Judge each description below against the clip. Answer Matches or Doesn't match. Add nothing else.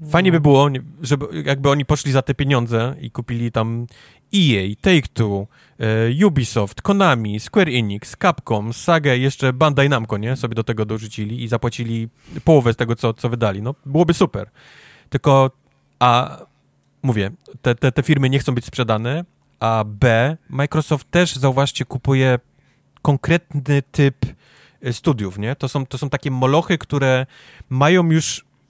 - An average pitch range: Matches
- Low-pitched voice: Matches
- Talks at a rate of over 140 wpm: Matches